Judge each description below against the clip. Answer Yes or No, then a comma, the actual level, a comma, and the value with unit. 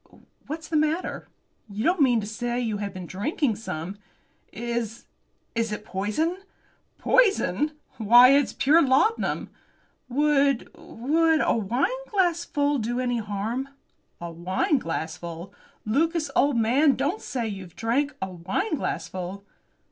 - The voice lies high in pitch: Yes, high, 240 Hz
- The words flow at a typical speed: No, slow, 120 wpm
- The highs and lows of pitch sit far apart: Yes, wide, 6.7 semitones